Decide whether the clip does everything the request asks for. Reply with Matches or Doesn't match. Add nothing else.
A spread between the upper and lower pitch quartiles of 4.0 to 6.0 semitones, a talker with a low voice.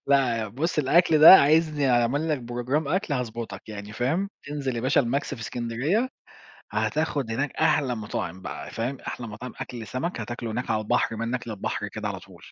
Matches